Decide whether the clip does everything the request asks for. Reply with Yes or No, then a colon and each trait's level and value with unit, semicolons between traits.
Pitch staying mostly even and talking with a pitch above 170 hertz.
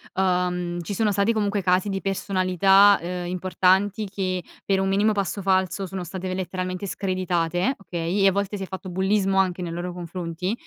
Yes: narrow, 1.5 semitones; high, 190 Hz